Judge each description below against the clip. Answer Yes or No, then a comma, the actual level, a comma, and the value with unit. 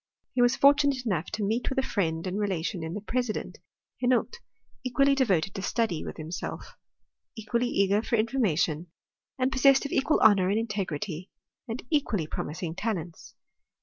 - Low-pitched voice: No, high, 215 Hz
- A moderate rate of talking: Yes, average, 155 wpm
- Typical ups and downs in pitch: No, wide, 5.9 semitones